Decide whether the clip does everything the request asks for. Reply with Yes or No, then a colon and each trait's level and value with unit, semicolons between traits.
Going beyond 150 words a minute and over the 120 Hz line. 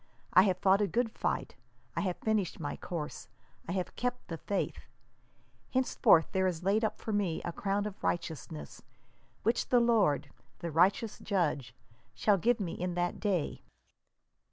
Yes: average, 160 wpm; high, 190 Hz